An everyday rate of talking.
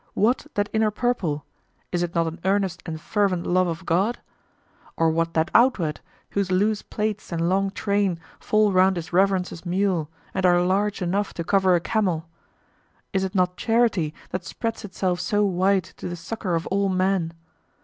Yes: average, 175 wpm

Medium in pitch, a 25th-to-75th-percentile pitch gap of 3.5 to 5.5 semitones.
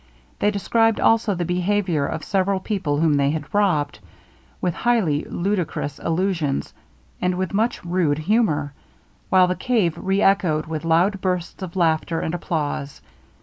Yes: medium, 180 Hz; average, 3.9 semitones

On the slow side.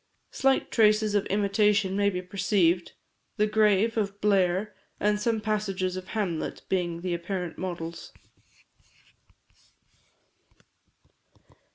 Yes: slow, 100 wpm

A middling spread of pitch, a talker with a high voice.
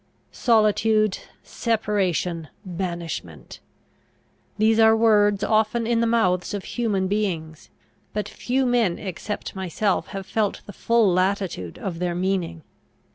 Yes: average, 3.6 semitones; high, 200 Hz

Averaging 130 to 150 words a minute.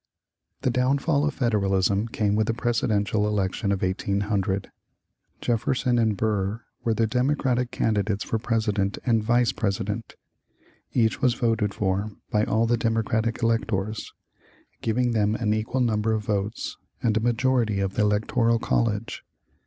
Yes: average, 140 wpm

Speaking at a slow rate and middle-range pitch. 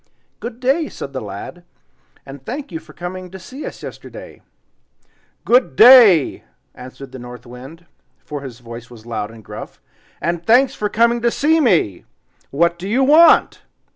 No: average, 165 wpm; medium, 175 Hz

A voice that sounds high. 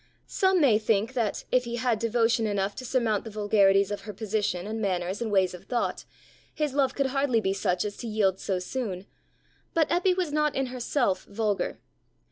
Yes: high, 220 Hz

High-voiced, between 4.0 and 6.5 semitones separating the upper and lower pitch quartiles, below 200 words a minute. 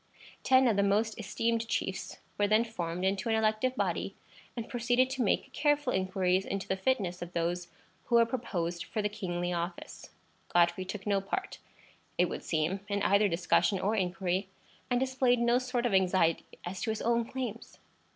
Yes: high, 205 Hz; average, 4.3 semitones; average, 180 wpm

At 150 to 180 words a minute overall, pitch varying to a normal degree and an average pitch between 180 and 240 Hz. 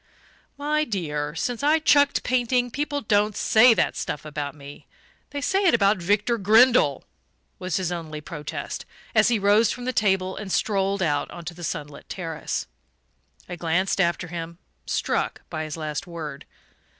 No: average, 160 wpm; wide, 6.4 semitones; high, 190 Hz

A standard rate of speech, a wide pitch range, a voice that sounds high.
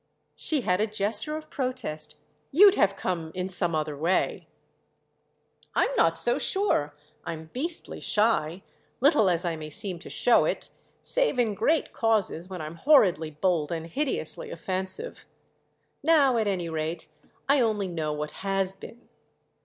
Yes: average, 145 wpm; wide, 7.5 semitones; high, 195 Hz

